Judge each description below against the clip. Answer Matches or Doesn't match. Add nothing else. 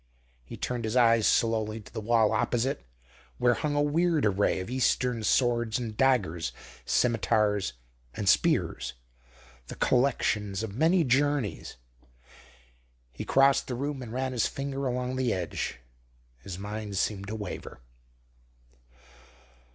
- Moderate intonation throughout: Matches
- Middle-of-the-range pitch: Doesn't match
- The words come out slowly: Matches